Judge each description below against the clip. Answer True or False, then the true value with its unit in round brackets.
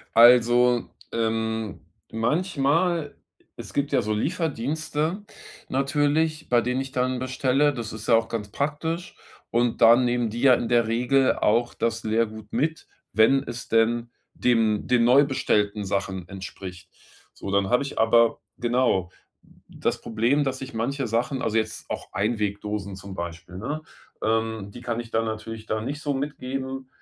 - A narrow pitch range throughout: False (3.6 semitones)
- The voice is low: True (120 Hz)